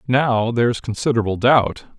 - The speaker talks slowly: Yes, slow, 120 wpm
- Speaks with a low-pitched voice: Yes, low, 120 Hz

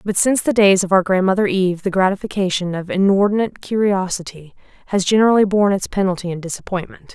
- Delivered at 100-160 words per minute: No, average, 170 wpm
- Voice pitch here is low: No, high, 190 Hz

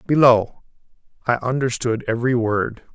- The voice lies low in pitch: Yes, low, 120 Hz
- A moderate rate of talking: No, slow, 100 wpm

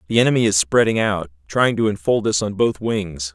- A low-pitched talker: Yes, low, 100 Hz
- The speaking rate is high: Yes, fast, 215 wpm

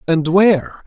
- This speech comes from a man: Yes, male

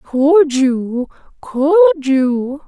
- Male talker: No, female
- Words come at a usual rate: No, slow, 90 wpm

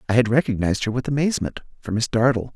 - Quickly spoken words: Yes, fast, 210 wpm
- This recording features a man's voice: Yes, male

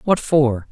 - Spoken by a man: Yes, male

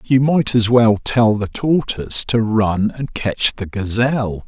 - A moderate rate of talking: Yes, average, 175 wpm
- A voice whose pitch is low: Yes, low, 115 Hz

